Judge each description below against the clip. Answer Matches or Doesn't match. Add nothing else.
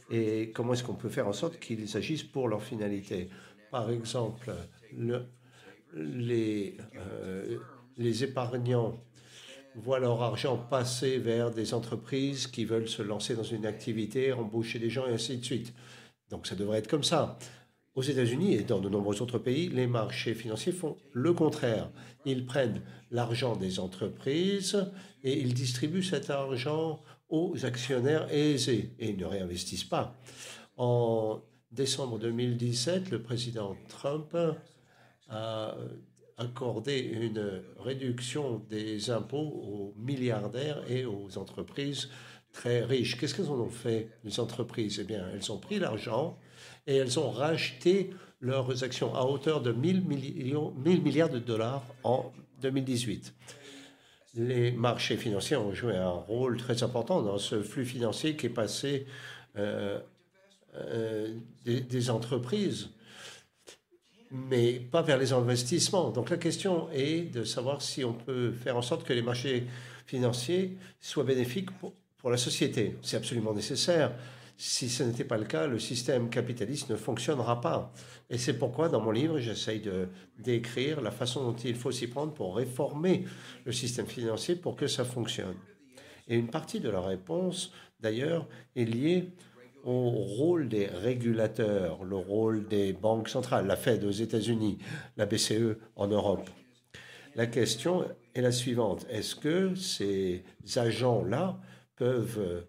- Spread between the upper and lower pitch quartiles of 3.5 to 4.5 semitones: Matches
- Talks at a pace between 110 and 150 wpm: Matches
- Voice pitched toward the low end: Matches